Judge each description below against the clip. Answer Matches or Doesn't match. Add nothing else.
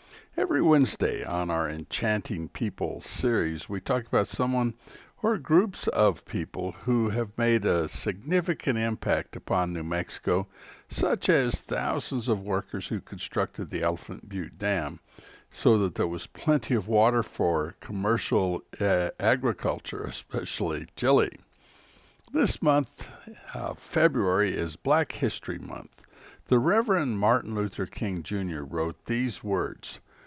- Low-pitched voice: Matches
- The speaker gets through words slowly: Matches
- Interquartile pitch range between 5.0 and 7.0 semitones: Matches